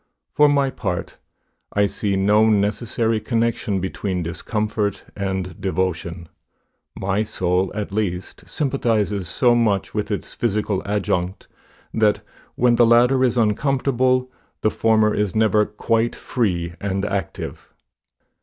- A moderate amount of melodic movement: Yes, average, 3.3 semitones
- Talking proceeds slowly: Yes, slow, 120 wpm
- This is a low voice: Yes, low, 105 Hz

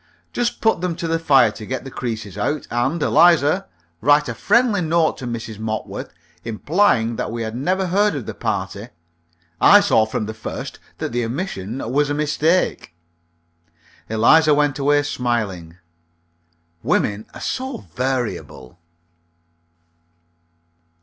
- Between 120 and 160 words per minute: Yes, slow, 135 wpm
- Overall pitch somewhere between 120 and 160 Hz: Yes, low, 135 Hz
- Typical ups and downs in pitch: No, wide, 6.8 semitones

